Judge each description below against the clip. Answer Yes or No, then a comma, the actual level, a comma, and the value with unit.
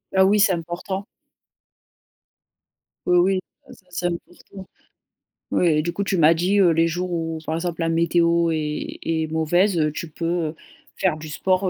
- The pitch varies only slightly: Yes, narrow, 2.2 semitones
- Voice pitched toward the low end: No, medium, 170 Hz